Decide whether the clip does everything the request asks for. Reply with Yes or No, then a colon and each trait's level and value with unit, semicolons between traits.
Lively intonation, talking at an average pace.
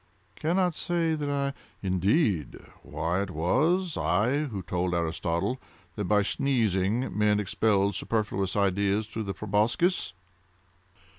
No: wide, 6.8 semitones; slow, 115 wpm